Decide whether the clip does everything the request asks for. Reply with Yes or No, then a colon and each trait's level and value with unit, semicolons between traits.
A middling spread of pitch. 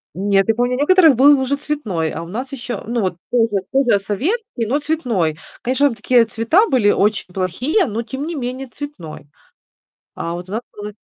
No: wide, 5.8 semitones